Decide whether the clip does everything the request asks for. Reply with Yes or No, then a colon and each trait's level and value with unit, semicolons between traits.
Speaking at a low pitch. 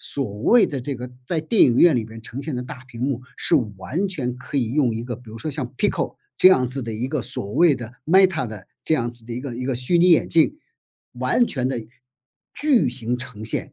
Yes: low, 125 Hz